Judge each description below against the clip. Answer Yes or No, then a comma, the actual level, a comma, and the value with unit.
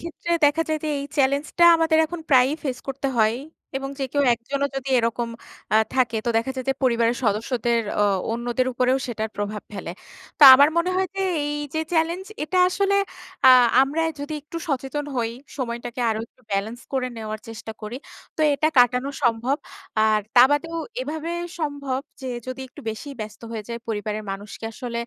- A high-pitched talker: Yes, very high, 255 Hz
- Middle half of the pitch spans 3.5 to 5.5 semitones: Yes, average, 4.1 semitones